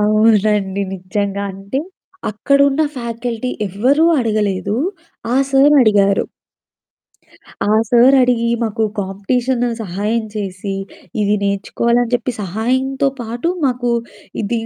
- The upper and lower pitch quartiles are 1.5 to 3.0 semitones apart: No, average, 3.7 semitones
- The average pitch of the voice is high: Yes, high, 225 Hz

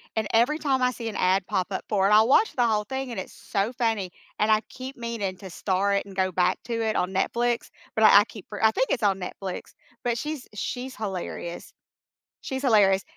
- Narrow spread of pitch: No, average, 3.9 semitones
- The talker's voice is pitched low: No, high, 215 Hz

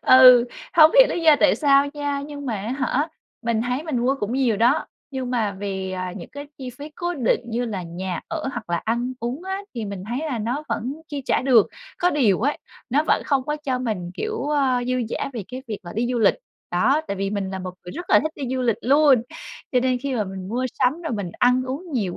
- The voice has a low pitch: No, very high, 250 Hz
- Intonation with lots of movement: No, average, 4.9 semitones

